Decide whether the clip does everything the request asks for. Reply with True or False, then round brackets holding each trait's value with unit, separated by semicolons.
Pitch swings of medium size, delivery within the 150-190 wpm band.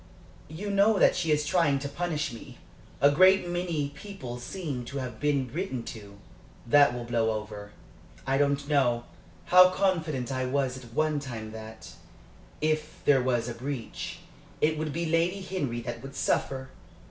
True (5.0 semitones; 165 wpm)